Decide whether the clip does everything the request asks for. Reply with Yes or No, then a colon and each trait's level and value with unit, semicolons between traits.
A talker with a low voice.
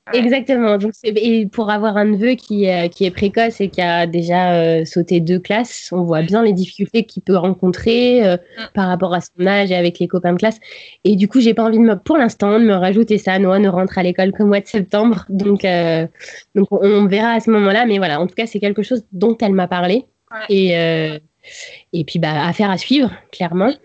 No: high, 200 Hz